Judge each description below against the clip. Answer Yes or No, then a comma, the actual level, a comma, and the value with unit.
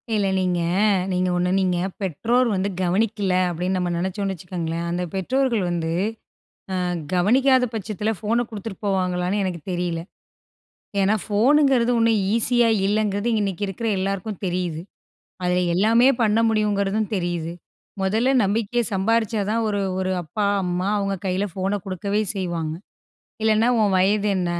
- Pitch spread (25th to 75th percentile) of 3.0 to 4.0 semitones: Yes, average, 3.4 semitones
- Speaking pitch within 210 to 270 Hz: No, high, 195 Hz